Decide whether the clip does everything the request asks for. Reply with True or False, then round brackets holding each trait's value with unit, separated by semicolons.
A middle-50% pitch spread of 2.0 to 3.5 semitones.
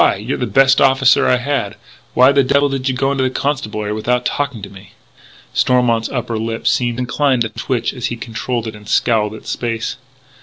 True (2.9 semitones)